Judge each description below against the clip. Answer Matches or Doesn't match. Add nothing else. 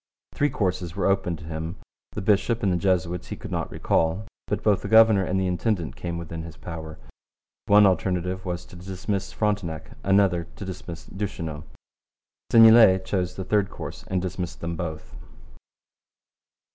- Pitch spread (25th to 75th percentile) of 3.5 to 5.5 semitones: Doesn't match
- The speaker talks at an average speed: Matches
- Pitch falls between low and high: Doesn't match